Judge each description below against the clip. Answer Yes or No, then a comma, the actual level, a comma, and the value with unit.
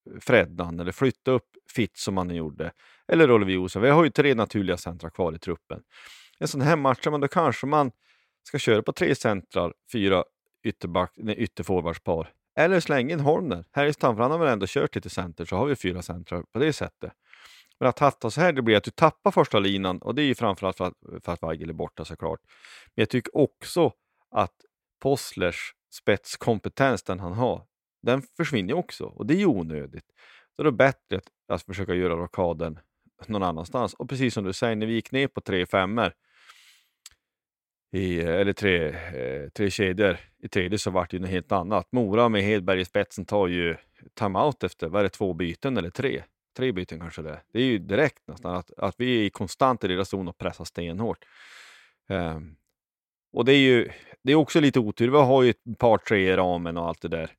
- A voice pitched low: Yes, low, 100 Hz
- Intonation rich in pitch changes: Yes, wide, 6.0 semitones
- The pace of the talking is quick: Yes, fast, 205 wpm